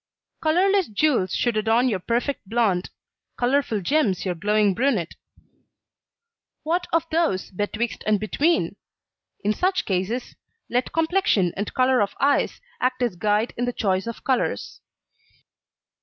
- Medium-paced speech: No, slow, 130 wpm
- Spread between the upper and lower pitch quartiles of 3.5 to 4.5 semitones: No, wide, 5.6 semitones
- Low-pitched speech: No, high, 235 Hz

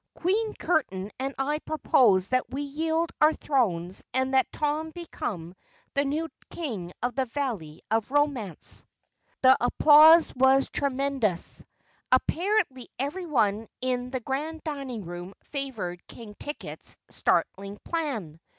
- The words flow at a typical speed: No, slow, 125 wpm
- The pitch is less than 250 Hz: No, very high, 265 Hz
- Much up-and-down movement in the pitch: Yes, wide, 5.9 semitones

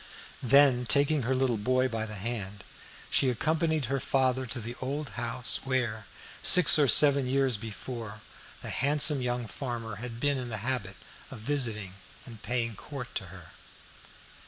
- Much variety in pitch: No, average, 3.2 semitones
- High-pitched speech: No, low, 125 Hz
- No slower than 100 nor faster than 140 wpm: No, average, 160 wpm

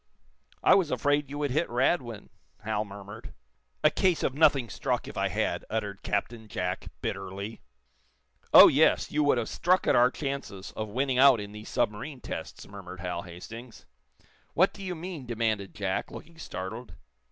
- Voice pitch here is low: Yes, low, 115 Hz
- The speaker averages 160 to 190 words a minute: Yes, average, 165 wpm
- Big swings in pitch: Yes, wide, 5.8 semitones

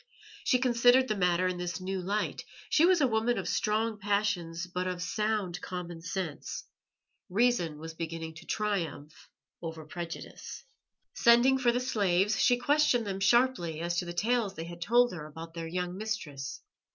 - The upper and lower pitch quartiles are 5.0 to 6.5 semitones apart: Yes, average, 5.3 semitones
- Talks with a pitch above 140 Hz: Yes, high, 190 Hz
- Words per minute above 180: No, average, 165 wpm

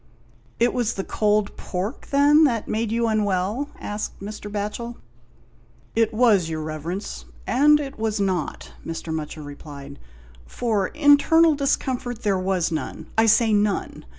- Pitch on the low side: No, high, 210 Hz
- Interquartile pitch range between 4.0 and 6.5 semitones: Yes, average, 4.7 semitones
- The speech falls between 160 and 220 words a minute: No, average, 150 wpm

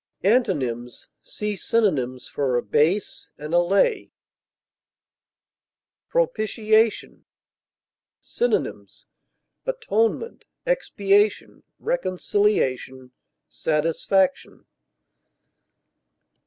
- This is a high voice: Yes, high, 200 Hz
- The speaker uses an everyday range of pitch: No, wide, 7.1 semitones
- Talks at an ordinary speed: No, slow, 45 wpm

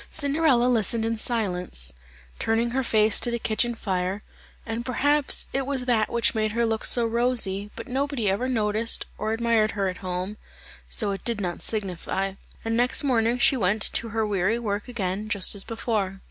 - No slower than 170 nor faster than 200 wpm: Yes, average, 180 wpm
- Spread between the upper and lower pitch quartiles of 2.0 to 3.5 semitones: Yes, average, 2.9 semitones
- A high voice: Yes, high, 225 Hz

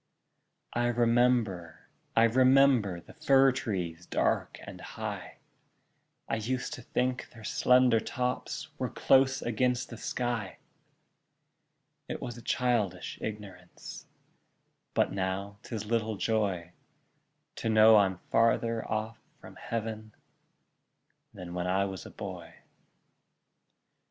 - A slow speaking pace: Yes, slow, 110 wpm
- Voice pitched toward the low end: Yes, low, 115 Hz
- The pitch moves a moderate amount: Yes, average, 3.7 semitones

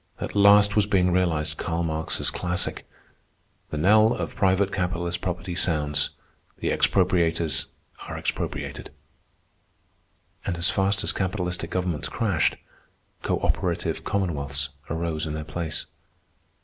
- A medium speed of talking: No, slow, 115 wpm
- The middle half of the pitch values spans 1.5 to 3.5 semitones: Yes, average, 3.2 semitones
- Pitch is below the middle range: Yes, very low, 90 Hz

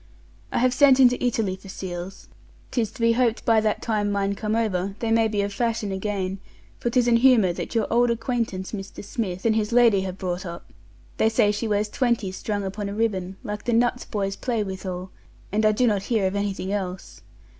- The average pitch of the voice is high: Yes, high, 210 Hz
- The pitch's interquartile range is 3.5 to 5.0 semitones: No, average, 3.1 semitones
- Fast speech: Yes, fast, 210 wpm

